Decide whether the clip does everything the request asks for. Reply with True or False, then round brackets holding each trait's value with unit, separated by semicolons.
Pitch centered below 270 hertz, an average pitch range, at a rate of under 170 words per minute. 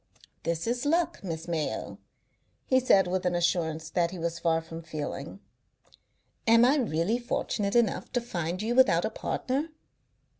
False (185 Hz; 6.4 semitones; 155 wpm)